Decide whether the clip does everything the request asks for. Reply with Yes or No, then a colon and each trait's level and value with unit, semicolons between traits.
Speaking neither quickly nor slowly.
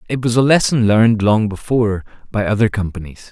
Yes: average, 180 wpm